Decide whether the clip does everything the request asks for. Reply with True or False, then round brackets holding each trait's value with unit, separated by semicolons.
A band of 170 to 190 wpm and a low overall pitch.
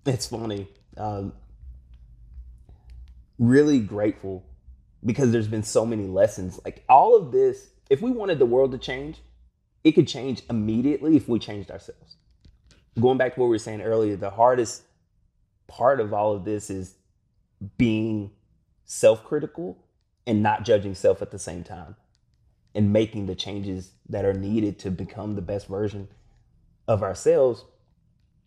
False (150 wpm; 105 Hz)